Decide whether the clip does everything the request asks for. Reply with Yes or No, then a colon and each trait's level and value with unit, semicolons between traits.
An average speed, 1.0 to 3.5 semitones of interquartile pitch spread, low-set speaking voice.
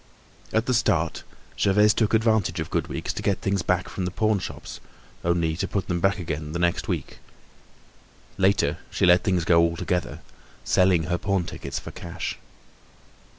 Yes: average, 170 wpm; average, 2.7 semitones; very low, 90 Hz